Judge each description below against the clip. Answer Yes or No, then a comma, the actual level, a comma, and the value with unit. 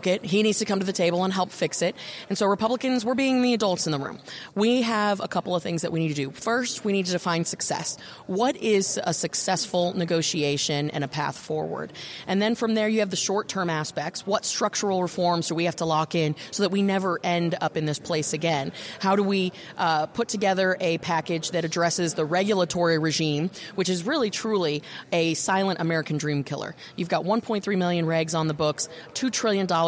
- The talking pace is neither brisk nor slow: No, fast, 220 wpm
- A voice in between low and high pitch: Yes, medium, 180 Hz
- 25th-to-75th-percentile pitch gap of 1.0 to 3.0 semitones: No, average, 3.7 semitones